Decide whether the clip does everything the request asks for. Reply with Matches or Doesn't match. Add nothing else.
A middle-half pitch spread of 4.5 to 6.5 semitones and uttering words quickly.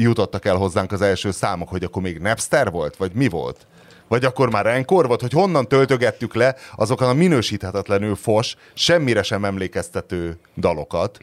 Matches